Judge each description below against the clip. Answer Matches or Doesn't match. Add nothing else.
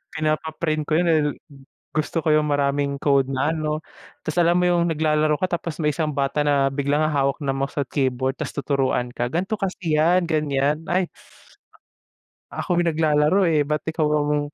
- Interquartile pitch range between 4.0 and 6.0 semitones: Doesn't match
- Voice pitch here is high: Doesn't match